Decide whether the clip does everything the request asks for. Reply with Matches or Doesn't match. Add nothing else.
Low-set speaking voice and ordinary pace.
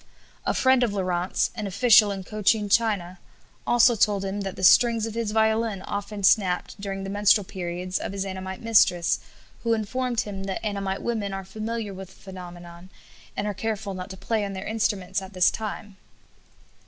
Doesn't match